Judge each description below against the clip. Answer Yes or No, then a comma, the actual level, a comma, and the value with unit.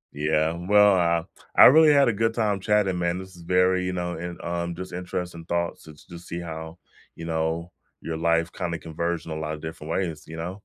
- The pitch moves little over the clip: Yes, narrow, 2.0 semitones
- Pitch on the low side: Yes, very low, 85 Hz